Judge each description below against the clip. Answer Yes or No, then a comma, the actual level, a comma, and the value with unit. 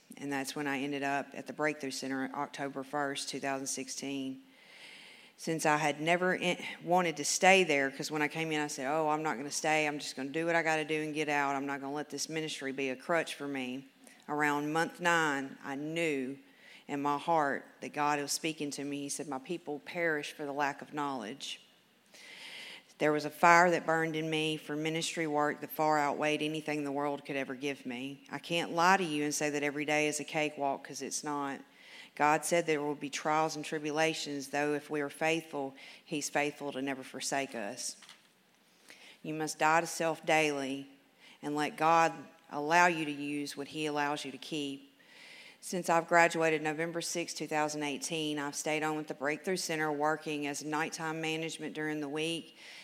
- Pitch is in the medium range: Yes, medium, 150 Hz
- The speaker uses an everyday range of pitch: No, narrow, 1.9 semitones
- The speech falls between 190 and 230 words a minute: Yes, fast, 205 wpm